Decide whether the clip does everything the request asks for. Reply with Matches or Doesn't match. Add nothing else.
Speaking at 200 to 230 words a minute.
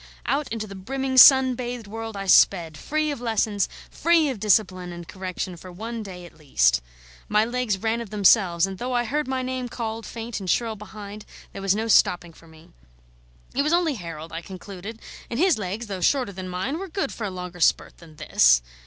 Matches